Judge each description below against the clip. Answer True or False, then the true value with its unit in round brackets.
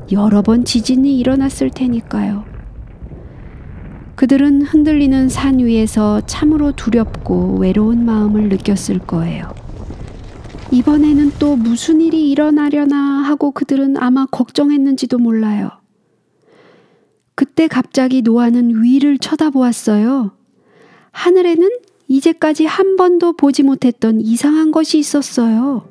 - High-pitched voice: True (265 Hz)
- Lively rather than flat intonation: False (4.2 semitones)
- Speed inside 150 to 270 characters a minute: True (265 characters per minute)